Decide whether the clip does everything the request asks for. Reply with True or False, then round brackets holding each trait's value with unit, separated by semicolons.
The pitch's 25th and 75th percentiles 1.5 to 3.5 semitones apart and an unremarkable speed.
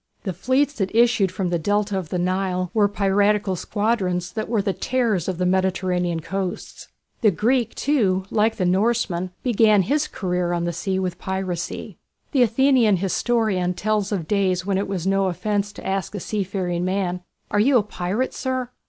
True (3.0 semitones; 180 wpm)